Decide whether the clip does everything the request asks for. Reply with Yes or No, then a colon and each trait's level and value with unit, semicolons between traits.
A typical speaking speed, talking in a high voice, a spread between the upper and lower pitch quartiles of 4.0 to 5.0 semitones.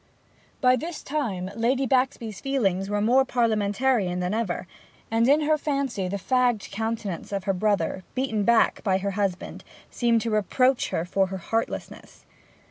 Yes: average, 150 wpm; high, 225 Hz; average, 4.6 semitones